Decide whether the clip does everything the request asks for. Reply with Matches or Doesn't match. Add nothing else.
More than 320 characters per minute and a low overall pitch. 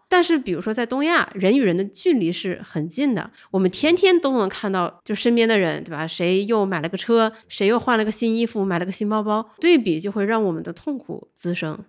Doesn't match